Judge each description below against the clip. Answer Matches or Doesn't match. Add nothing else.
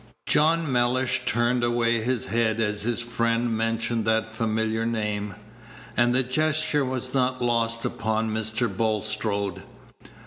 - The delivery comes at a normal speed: Doesn't match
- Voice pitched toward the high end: Doesn't match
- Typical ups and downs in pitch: Doesn't match